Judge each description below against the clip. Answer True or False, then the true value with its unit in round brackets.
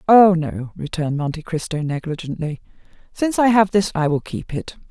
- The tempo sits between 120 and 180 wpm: True (170 wpm)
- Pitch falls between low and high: True (170 Hz)